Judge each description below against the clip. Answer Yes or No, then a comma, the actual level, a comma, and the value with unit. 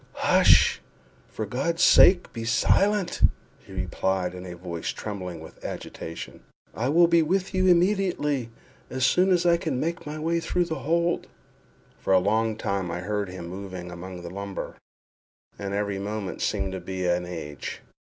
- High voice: No, low, 105 Hz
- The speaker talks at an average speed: Yes, average, 160 wpm